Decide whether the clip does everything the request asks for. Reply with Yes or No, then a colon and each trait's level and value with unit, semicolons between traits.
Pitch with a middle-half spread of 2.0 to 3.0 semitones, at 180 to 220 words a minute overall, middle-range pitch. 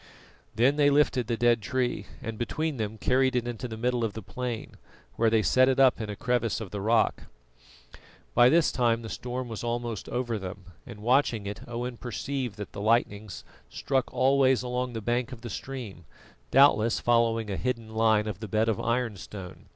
No: narrow, 2.5 semitones; average, 190 wpm; low, 120 Hz